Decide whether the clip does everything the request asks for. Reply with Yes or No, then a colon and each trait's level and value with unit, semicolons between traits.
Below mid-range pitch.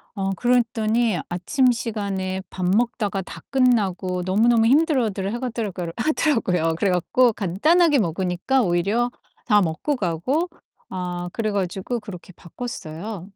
No: high, 205 Hz